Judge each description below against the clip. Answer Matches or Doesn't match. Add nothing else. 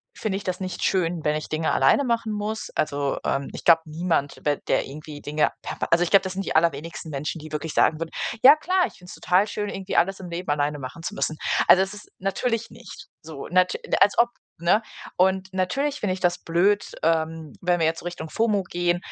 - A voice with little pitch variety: Doesn't match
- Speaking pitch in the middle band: Matches